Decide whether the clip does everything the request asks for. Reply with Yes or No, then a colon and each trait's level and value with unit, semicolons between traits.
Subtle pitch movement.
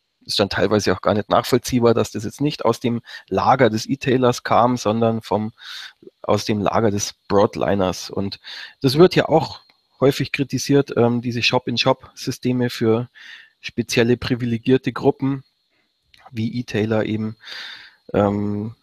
No: average, 3.3 semitones